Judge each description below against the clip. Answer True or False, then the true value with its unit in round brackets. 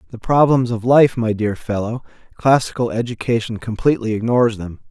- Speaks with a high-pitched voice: False (115 Hz)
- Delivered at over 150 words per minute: False (135 wpm)